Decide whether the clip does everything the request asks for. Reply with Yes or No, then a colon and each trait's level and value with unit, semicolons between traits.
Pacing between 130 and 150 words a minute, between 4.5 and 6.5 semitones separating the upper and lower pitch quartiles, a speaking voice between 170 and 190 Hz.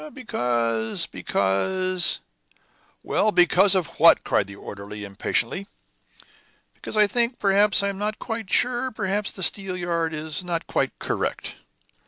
Yes: slow, 135 wpm; wide, 5.5 semitones; medium, 185 Hz